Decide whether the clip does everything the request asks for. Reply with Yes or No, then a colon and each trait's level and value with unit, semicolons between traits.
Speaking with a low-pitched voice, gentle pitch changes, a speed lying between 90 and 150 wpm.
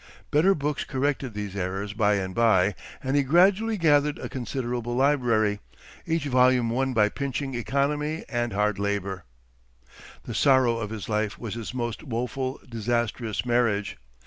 No: low, 120 Hz; average, 4.5 semitones; average, 145 wpm